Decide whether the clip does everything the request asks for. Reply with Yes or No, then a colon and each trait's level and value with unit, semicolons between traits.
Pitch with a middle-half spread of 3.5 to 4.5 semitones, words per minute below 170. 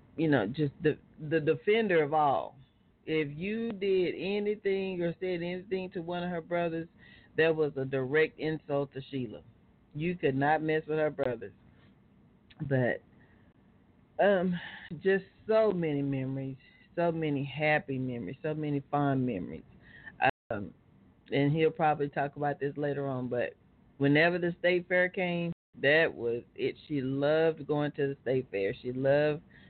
Yes: average, 3.8 semitones; average, 150 wpm